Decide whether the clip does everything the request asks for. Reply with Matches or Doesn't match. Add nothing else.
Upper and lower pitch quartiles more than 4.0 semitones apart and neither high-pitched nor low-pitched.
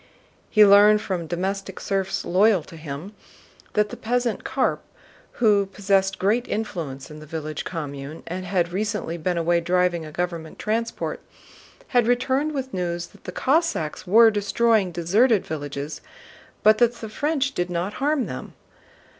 Doesn't match